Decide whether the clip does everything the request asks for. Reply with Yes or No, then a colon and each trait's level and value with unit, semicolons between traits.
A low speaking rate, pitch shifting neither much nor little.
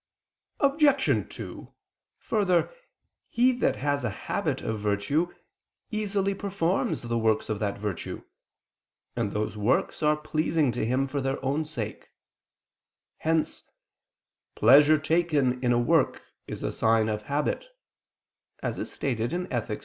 No: slow, 120 wpm; wide, 7.1 semitones